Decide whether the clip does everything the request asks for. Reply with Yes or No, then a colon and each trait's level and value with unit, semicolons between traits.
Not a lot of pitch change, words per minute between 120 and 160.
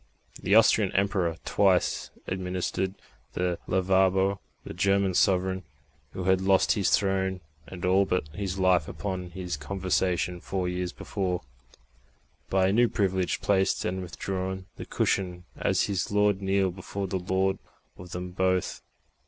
Yes: narrow, 1.2 semitones; average, 140 wpm